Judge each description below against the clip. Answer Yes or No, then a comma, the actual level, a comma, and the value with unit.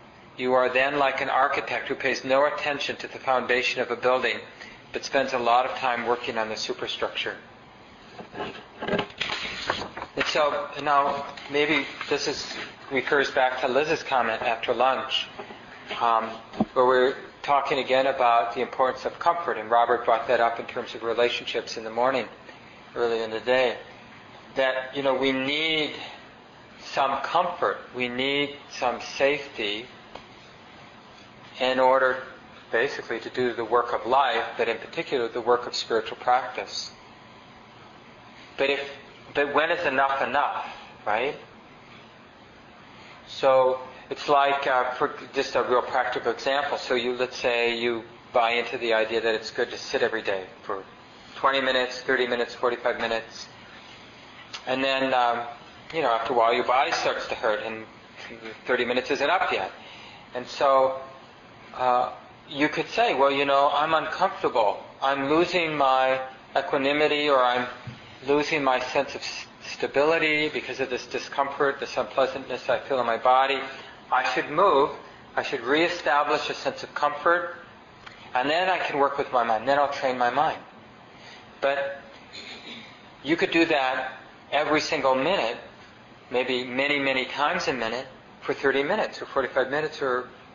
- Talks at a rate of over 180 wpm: No, average, 155 wpm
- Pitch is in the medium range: No, low, 130 Hz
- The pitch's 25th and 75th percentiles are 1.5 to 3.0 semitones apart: Yes, narrow, 2.4 semitones